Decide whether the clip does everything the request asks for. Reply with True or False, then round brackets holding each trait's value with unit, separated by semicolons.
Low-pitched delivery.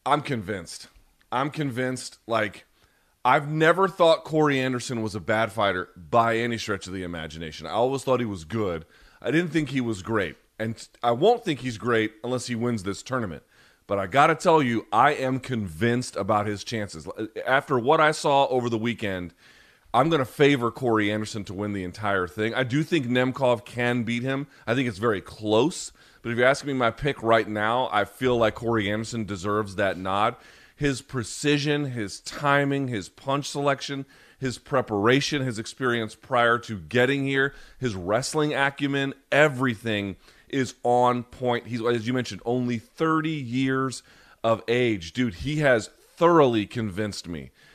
True (120 Hz)